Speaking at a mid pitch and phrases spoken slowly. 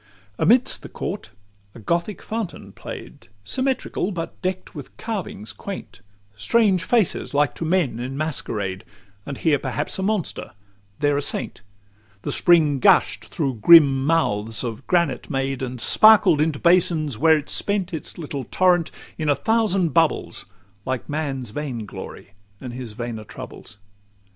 No: medium, 150 Hz; average, 150 wpm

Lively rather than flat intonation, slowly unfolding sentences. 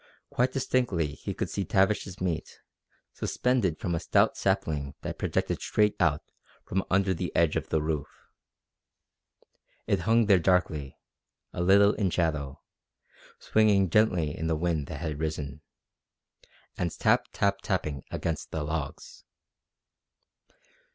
No: average, 4.3 semitones; slow, 130 wpm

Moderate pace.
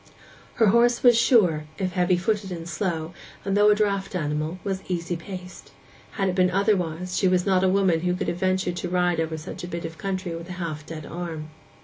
No: fast, 220 wpm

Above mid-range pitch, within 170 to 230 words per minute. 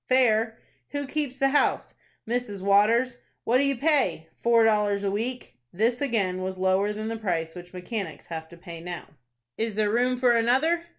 Yes: high, 220 Hz; average, 180 wpm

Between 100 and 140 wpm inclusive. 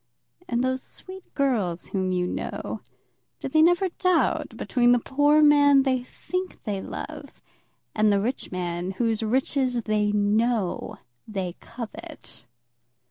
Yes: slow, 135 wpm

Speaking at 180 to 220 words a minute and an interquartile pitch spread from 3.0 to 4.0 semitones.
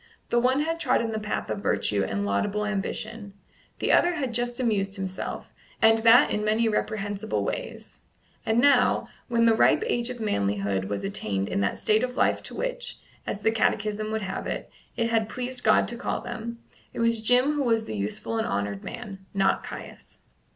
Yes: average, 190 wpm; average, 3.4 semitones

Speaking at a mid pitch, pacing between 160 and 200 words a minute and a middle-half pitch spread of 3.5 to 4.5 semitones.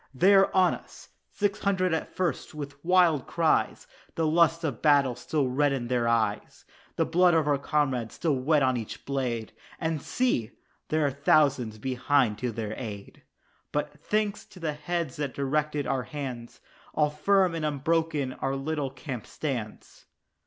Yes: medium, 145 Hz; average, 165 wpm; average, 4.1 semitones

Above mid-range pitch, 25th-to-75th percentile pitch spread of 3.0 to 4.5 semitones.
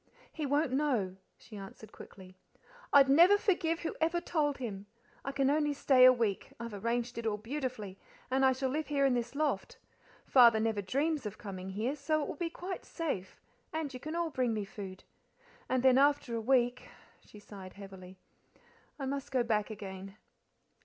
No: very high, 255 Hz; wide, 5.6 semitones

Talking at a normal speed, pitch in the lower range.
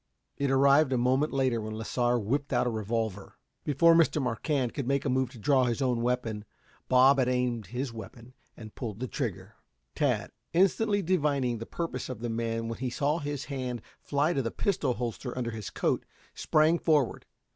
Yes: average, 190 wpm; low, 125 Hz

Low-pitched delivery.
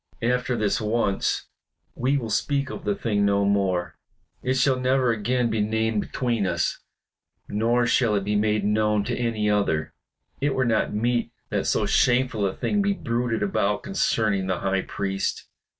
Yes: low, 110 Hz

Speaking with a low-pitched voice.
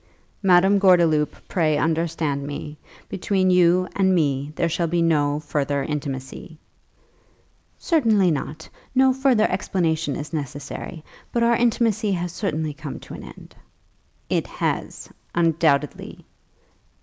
No: medium, 165 Hz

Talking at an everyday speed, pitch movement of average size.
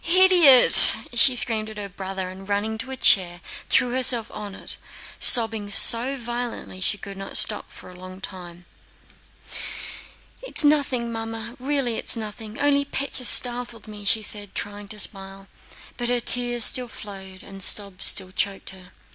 Yes: average, 165 wpm; average, 4.0 semitones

